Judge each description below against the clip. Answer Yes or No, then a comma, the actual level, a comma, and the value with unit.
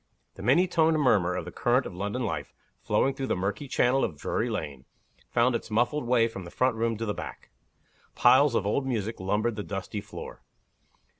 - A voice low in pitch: Yes, low, 115 Hz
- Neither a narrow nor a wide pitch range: Yes, average, 4.2 semitones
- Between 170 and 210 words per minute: Yes, average, 200 wpm